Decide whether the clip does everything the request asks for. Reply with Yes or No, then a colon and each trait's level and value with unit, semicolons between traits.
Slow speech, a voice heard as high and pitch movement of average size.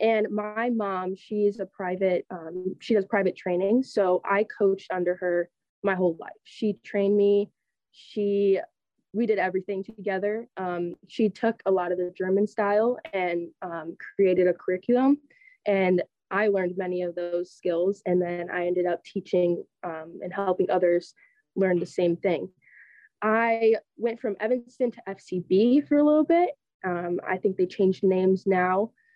No: average, 165 wpm; high, 195 Hz; average, 3.1 semitones